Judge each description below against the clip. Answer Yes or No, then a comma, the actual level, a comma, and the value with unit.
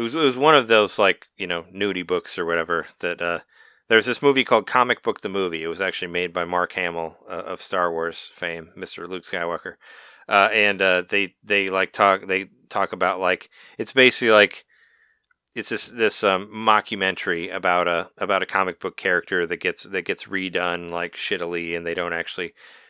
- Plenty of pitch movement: No, average, 3.2 semitones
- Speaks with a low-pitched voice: Yes, very low, 95 Hz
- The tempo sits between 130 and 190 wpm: No, average, 200 wpm